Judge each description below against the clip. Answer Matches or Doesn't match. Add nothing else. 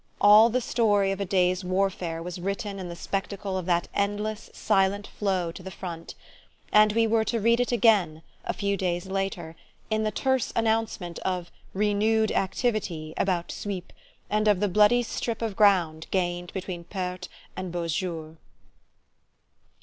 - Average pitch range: Matches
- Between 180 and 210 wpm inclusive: Doesn't match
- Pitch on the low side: Doesn't match